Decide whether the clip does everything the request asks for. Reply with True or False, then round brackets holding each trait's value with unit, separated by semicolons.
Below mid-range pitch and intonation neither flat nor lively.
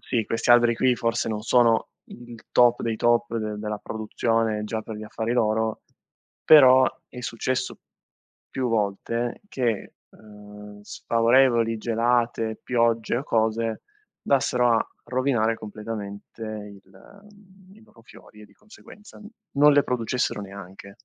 False (115 Hz; 2.2 semitones)